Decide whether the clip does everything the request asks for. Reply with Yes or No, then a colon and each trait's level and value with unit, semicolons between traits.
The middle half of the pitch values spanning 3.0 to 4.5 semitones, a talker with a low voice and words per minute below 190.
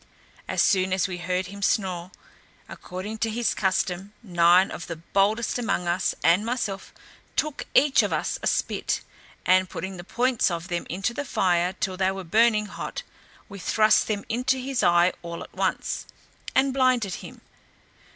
No: average, 3.9 semitones; high, 195 Hz; average, 170 wpm